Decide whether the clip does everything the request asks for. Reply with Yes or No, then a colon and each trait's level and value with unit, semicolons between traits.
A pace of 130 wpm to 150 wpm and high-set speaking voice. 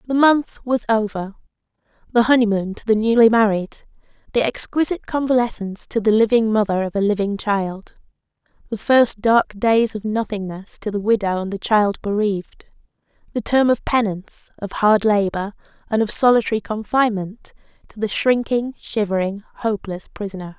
Yes: average, 145 wpm; high, 215 Hz